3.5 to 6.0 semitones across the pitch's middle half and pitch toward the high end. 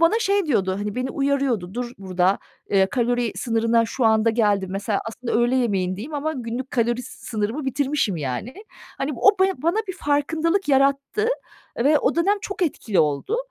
Yes: wide, 5.5 semitones; high, 245 Hz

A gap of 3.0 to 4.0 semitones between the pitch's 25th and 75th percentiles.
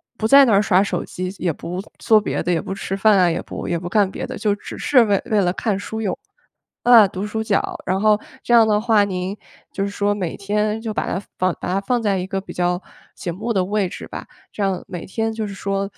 No: narrow, 2.6 semitones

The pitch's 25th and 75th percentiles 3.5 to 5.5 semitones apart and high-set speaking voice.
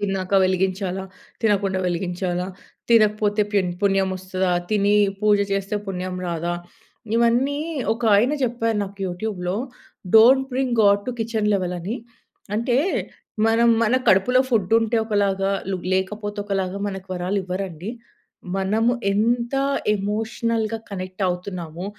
No: average, 3.1 semitones; high, 200 Hz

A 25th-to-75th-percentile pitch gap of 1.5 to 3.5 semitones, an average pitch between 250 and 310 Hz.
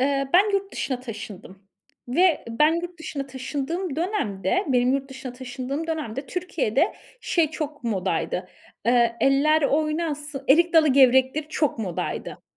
No: average, 4.2 semitones; very high, 275 Hz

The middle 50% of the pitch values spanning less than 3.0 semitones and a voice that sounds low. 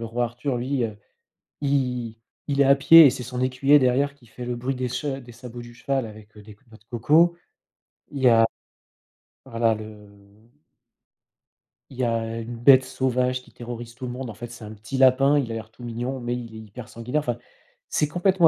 Yes: narrow, 2.6 semitones; low, 125 Hz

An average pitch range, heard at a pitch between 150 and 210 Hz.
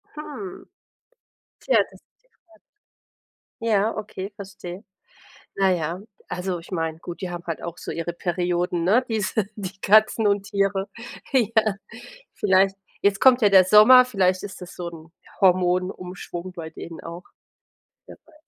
Yes: average, 3.0 semitones; high, 190 Hz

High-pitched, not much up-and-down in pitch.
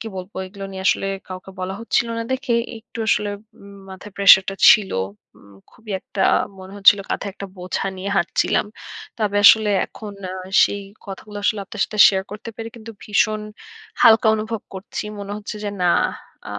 Yes: high, 205 Hz; narrow, 2.1 semitones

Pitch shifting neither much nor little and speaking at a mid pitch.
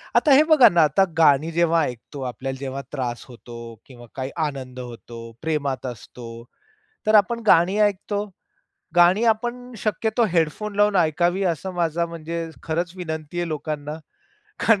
No: wide, 6.4 semitones; medium, 165 Hz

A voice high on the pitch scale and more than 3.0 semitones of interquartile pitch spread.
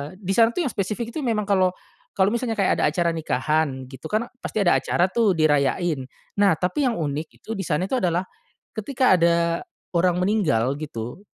No: medium, 180 Hz; average, 5.2 semitones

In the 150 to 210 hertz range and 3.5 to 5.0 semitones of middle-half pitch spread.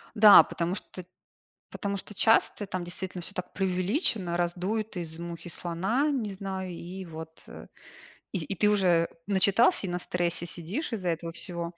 No: medium, 185 Hz; average, 2.9 semitones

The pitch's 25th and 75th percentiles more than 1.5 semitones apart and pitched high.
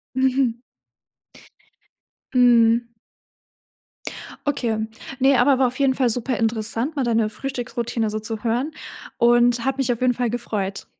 Yes: narrow, 2.4 semitones; high, 240 Hz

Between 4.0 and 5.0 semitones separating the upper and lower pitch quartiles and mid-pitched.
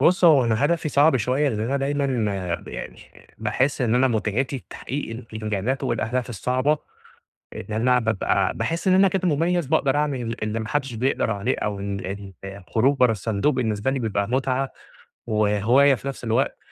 No: average, 4.3 semitones; low, 125 Hz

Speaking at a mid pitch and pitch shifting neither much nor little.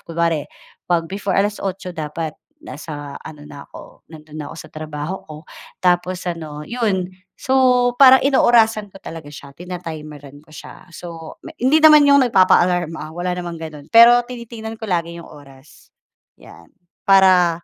No: medium, 175 Hz; wide, 5.9 semitones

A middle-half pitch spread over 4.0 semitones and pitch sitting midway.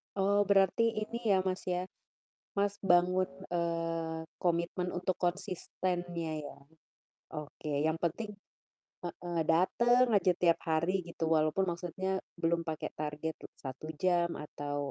No: narrow, 2.5 semitones; medium, 175 Hz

